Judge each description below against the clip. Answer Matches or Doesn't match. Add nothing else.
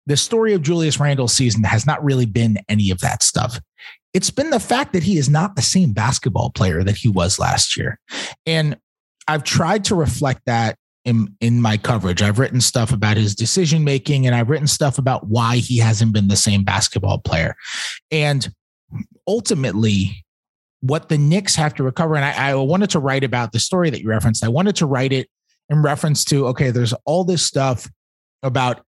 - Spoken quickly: Doesn't match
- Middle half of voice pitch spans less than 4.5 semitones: Doesn't match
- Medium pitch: Doesn't match